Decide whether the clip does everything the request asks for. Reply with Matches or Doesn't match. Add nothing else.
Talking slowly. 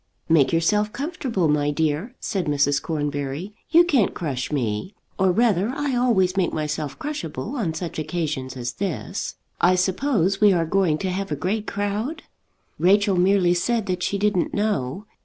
Doesn't match